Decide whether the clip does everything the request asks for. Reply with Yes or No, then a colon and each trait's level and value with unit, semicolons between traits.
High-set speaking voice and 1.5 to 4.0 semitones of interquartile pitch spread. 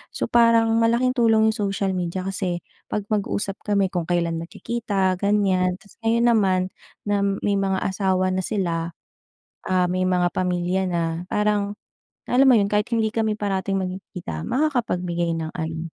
Yes: high, 195 Hz; average, 2.8 semitones